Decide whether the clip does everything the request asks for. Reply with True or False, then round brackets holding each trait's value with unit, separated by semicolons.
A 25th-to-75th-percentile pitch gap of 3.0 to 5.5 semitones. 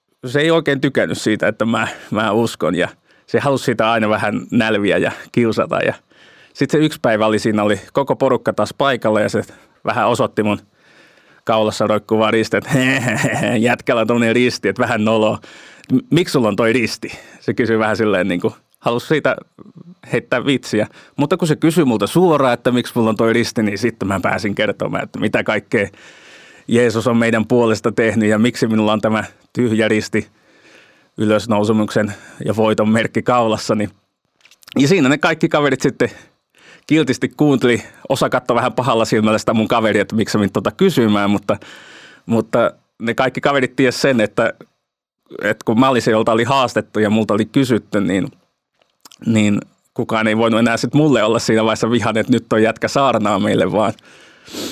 False (2.6 semitones)